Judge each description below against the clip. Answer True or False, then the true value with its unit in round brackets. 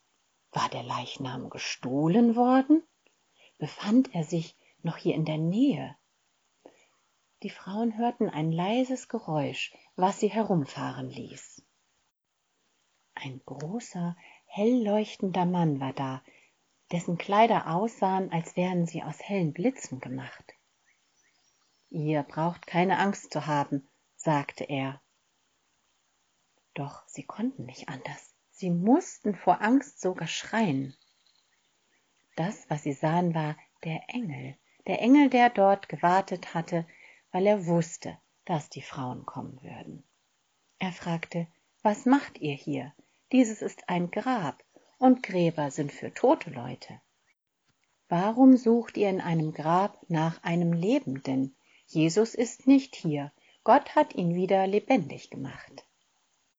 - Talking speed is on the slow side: True (120 wpm)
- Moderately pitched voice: True (175 Hz)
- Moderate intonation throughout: False (5.9 semitones)